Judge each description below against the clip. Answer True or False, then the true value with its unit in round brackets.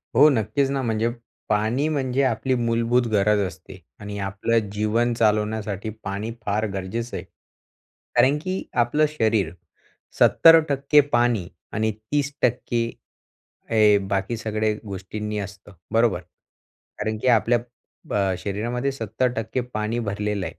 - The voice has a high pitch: False (110 Hz)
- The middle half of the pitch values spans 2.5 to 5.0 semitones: True (2.8 semitones)